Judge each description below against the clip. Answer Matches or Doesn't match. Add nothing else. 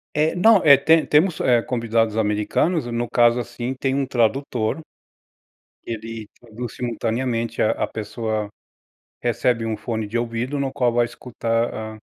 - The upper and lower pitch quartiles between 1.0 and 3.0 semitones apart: Matches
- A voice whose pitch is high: Doesn't match